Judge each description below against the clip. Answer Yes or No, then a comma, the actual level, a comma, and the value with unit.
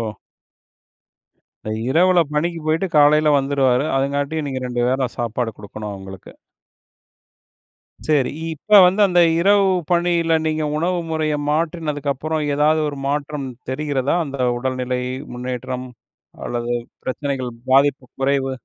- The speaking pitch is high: No, medium, 140 Hz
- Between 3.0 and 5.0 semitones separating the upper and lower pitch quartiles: Yes, average, 3.5 semitones